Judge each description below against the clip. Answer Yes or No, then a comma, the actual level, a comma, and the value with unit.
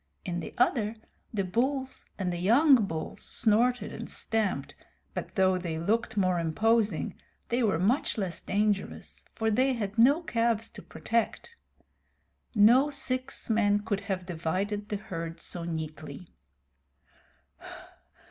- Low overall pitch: No, high, 210 Hz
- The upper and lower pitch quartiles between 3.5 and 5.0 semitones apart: Yes, average, 4.3 semitones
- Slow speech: Yes, slow, 130 wpm